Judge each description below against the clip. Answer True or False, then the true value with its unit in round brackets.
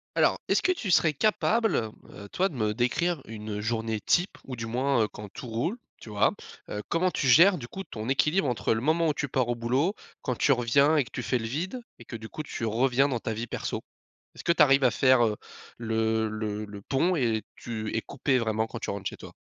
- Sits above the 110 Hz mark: True (125 Hz)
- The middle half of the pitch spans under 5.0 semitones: False (5.3 semitones)